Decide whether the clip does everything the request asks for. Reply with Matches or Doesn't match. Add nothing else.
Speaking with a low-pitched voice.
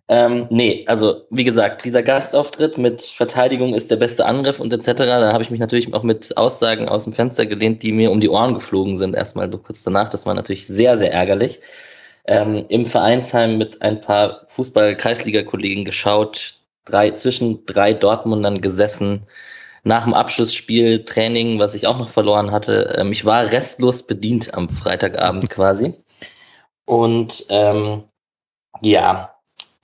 Matches